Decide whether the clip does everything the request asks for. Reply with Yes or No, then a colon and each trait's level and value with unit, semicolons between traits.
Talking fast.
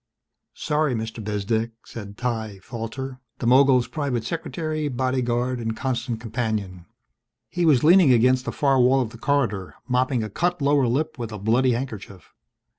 No: average, 160 wpm